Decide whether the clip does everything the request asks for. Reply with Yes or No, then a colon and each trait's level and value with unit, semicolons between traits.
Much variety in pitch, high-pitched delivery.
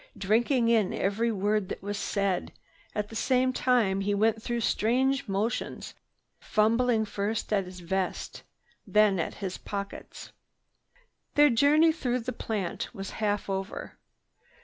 No: average, 3.3 semitones; high, 215 Hz